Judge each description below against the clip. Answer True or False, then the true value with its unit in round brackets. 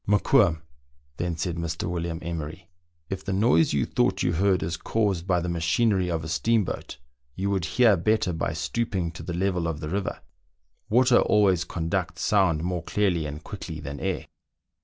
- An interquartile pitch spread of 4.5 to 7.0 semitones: False (3.1 semitones)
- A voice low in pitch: True (90 Hz)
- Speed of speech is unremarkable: True (180 wpm)